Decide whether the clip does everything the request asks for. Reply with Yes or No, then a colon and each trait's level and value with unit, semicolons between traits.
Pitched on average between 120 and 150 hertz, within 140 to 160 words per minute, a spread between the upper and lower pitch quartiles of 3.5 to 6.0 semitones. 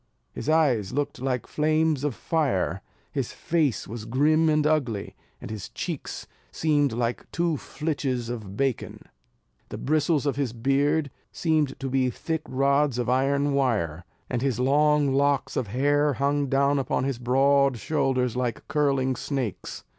No: low, 135 Hz; average, 150 wpm; average, 2.9 semitones